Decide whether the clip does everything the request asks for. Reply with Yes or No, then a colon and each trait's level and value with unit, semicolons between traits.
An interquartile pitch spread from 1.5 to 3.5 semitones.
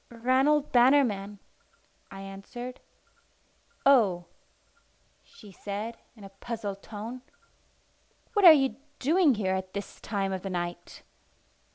No: average, 4.7 semitones